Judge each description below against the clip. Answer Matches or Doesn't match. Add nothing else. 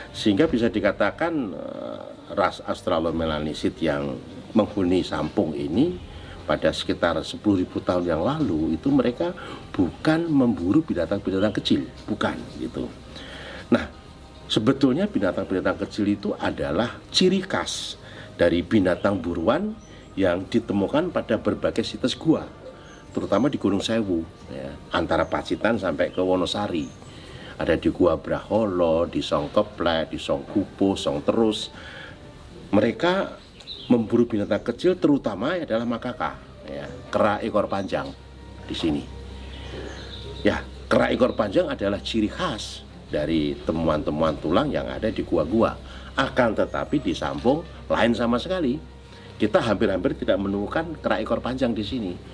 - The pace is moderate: Matches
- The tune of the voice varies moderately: Doesn't match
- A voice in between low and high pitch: Doesn't match